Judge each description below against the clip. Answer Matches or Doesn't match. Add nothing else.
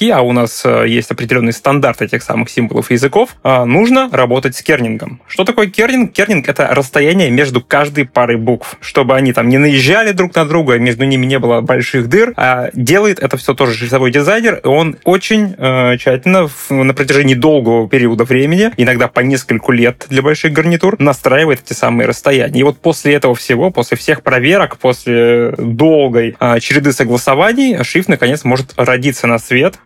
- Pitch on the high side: Doesn't match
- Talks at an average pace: Doesn't match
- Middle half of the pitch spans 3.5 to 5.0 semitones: Matches